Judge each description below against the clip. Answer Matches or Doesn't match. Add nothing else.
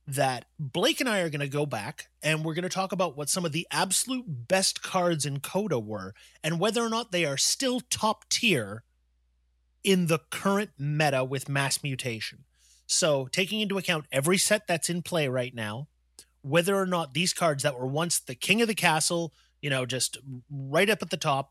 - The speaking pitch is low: Doesn't match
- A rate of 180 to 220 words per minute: Matches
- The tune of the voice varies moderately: Doesn't match